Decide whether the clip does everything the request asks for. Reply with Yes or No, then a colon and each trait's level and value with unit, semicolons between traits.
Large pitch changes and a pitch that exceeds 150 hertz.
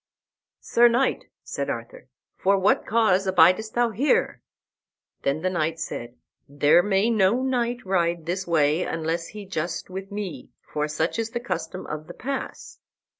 Yes: wide, 5.7 semitones; high, 190 Hz